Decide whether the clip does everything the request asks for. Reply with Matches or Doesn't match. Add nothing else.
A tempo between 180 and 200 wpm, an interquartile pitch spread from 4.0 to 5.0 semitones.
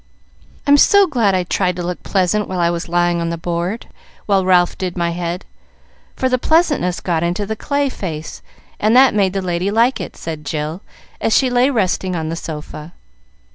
Matches